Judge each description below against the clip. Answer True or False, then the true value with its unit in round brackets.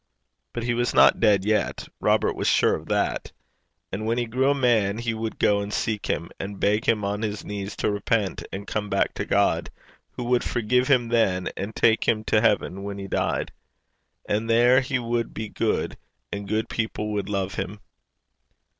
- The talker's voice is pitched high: False (110 Hz)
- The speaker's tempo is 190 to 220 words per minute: True (195 wpm)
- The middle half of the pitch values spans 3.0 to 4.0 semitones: False (2.6 semitones)